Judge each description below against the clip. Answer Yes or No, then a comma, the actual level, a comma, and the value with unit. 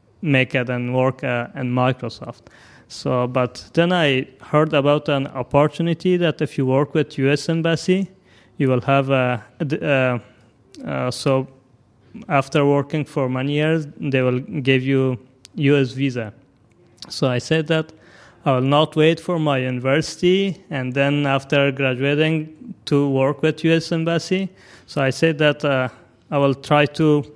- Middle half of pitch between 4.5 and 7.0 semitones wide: No, average, 3.3 semitones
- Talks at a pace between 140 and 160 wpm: Yes, average, 150 wpm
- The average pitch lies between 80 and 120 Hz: No, medium, 140 Hz